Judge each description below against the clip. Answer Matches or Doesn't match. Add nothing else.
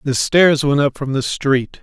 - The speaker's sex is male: Matches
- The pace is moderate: Doesn't match